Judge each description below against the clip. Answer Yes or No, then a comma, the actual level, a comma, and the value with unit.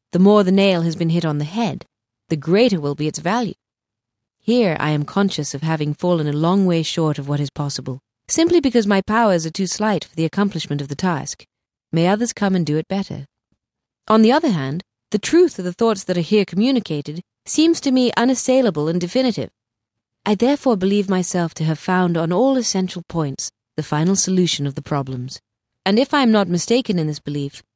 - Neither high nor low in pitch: Yes, medium, 175 Hz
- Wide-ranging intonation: Yes, wide, 6.0 semitones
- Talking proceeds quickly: Yes, fast, 210 wpm